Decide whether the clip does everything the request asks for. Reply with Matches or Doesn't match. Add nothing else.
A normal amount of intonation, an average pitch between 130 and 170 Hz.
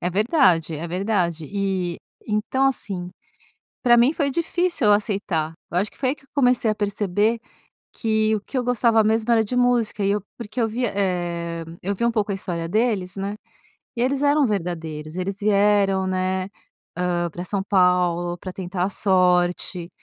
Doesn't match